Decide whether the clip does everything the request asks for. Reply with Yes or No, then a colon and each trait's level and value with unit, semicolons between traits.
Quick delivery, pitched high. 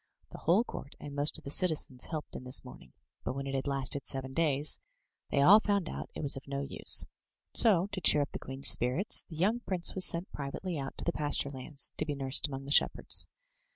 No: fast, 225 wpm; medium, 145 Hz